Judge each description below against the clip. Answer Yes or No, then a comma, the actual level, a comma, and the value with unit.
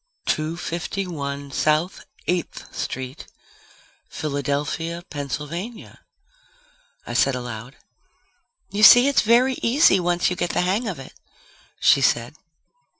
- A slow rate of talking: Yes, slow, 115 wpm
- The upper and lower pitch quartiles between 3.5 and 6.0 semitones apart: Yes, wide, 5.4 semitones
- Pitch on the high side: No, medium, 165 Hz